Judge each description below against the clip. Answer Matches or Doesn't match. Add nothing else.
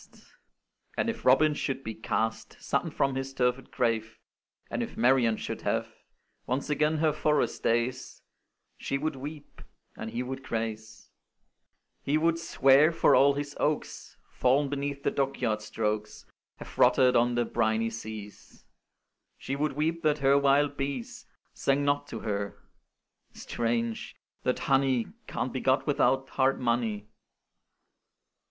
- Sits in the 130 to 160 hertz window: Matches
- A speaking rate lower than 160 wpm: Matches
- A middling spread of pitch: Matches